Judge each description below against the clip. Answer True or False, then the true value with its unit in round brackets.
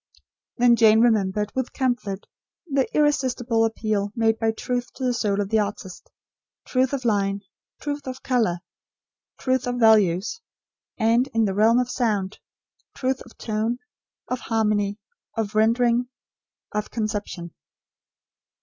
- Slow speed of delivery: True (130 wpm)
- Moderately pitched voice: False (225 Hz)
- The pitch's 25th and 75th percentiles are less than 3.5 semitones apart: True (3.0 semitones)